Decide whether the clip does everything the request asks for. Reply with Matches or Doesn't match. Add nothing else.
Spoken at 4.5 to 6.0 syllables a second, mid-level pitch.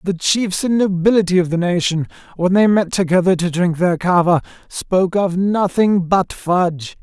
Matches